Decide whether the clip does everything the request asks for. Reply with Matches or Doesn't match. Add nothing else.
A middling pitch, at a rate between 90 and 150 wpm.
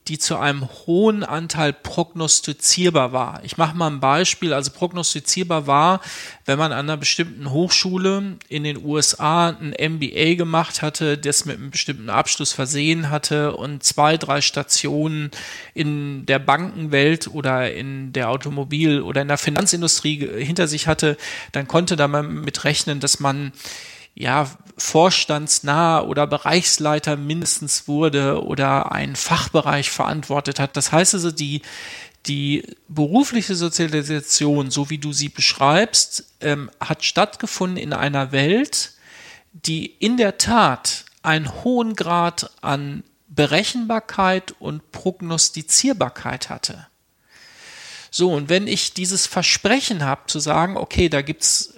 Matches